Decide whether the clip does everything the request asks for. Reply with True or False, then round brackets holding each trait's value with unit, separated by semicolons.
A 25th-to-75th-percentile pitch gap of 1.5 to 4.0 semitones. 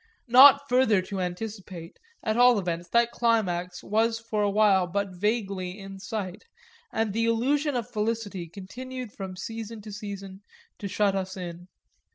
True (3.4 semitones)